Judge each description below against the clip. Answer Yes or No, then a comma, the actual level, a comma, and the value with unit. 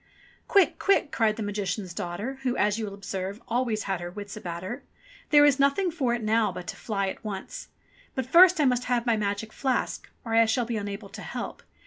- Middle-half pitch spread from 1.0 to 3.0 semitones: No, average, 4.2 semitones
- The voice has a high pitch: Yes, high, 220 Hz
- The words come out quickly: Yes, fast, 220 wpm